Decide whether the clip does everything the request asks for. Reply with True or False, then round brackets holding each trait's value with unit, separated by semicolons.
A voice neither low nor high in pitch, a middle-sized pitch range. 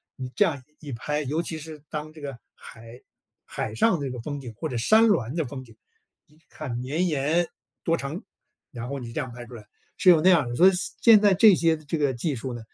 True (145 Hz; 4.9 semitones)